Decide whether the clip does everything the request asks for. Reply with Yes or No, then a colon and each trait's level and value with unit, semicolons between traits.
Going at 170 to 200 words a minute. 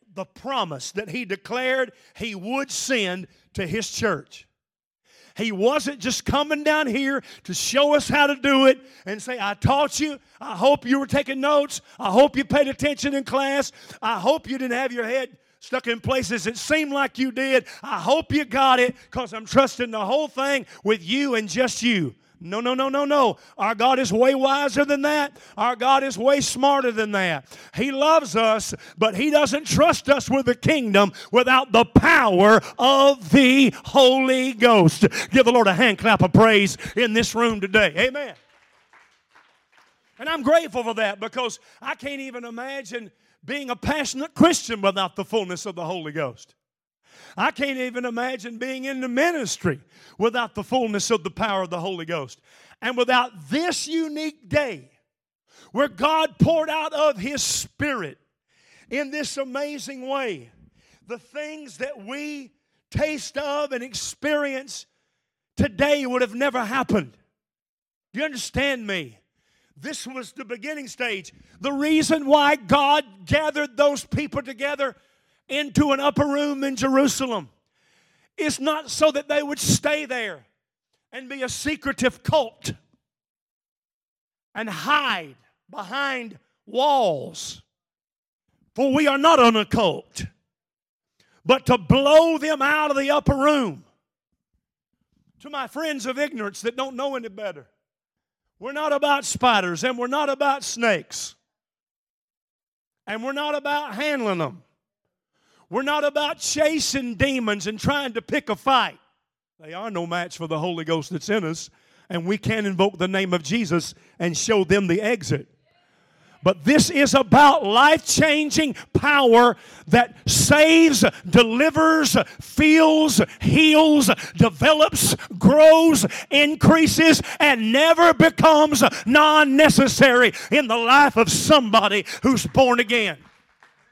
No: average, 150 wpm